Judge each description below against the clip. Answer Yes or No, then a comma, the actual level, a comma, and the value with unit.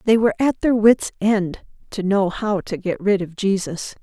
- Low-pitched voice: No, high, 200 Hz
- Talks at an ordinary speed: No, fast, 210 wpm